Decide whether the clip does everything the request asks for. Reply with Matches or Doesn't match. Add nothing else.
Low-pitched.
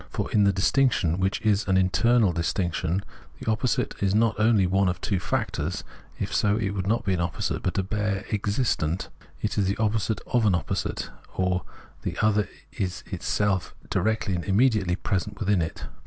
Matches